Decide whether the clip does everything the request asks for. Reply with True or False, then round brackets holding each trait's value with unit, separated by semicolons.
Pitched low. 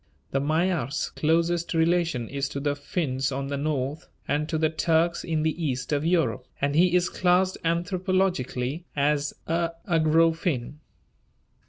False (160 Hz)